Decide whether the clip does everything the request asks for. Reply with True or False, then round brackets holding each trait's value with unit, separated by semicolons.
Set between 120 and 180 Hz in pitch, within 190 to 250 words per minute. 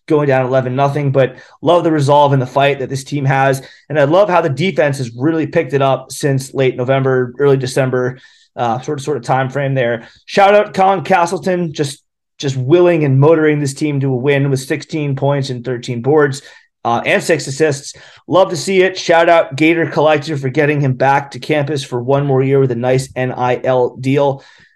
True (140 Hz; 205 wpm)